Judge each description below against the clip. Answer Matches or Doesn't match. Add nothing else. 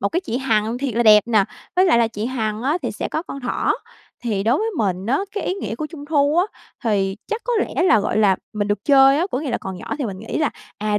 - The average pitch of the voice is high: Matches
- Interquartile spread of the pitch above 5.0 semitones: Matches